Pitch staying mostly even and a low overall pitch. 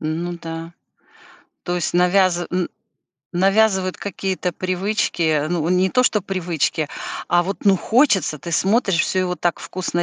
No: narrow, 2.0 semitones; medium, 180 Hz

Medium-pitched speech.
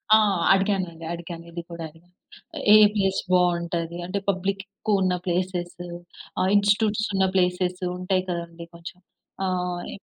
Yes: medium, 180 Hz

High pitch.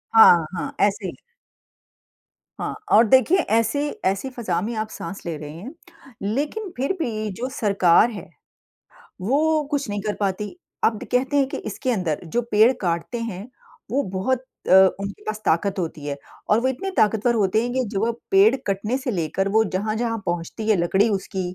Yes: high, 215 Hz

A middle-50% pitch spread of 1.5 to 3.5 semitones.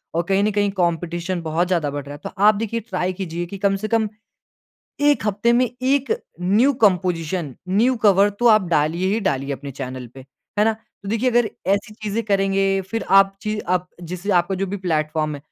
No: average, 4.0 semitones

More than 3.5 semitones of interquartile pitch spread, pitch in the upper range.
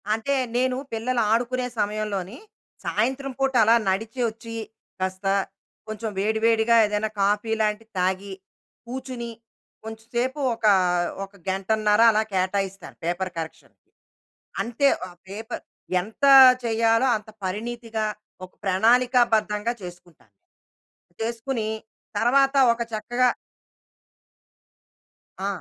No: average, 2.9 semitones; high, 220 Hz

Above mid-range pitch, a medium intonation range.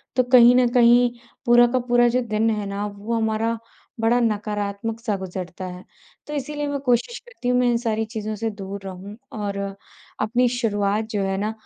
Yes: high, 225 Hz; average, 3.0 semitones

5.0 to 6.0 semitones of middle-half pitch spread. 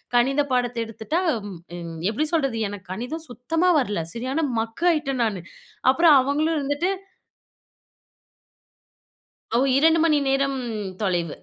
Yes: wide, 5.6 semitones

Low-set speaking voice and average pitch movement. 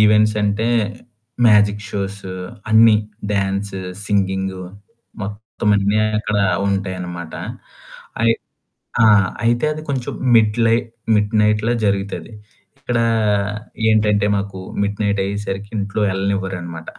No: low, 100 Hz; narrow, 1.6 semitones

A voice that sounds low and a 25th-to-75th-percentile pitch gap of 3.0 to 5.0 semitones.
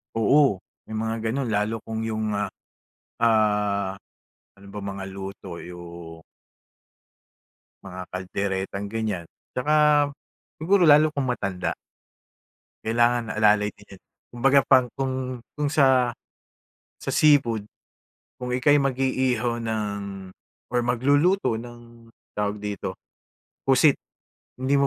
Yes: low, 115 Hz; average, 4.4 semitones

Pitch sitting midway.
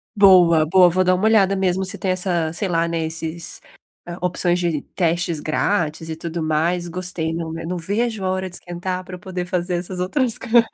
Yes: medium, 180 Hz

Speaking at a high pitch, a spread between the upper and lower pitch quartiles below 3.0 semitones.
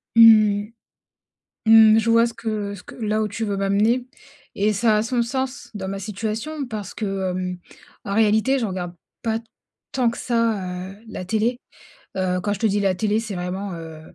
Yes: high, 210 Hz; narrow, 2.6 semitones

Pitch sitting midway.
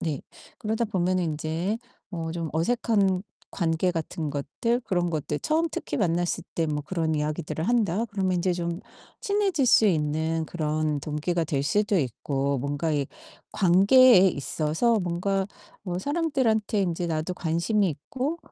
Yes: medium, 175 Hz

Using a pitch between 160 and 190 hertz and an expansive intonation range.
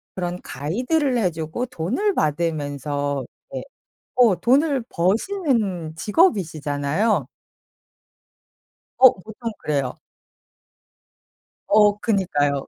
Yes: medium, 185 Hz; wide, 8.0 semitones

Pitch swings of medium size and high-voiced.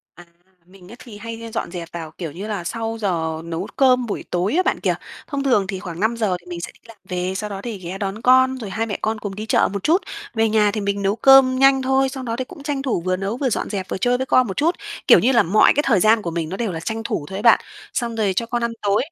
Yes: average, 4.6 semitones; high, 215 Hz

